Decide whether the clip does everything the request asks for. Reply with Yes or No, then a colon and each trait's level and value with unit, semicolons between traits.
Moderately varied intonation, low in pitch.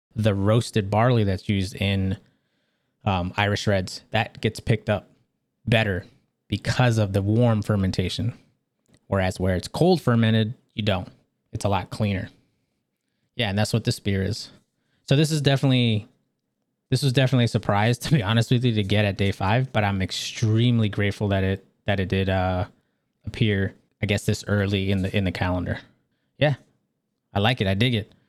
Yes: average, 3.3 semitones; low, 105 Hz